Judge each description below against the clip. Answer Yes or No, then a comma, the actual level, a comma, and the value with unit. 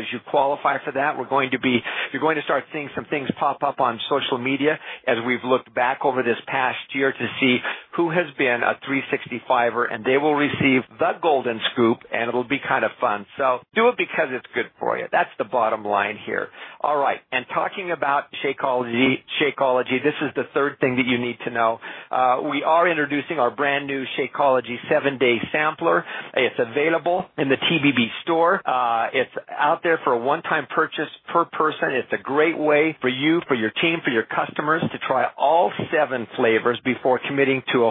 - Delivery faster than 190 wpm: Yes, fast, 205 wpm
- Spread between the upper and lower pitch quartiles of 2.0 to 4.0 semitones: Yes, average, 3.6 semitones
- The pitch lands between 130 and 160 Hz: Yes, low, 135 Hz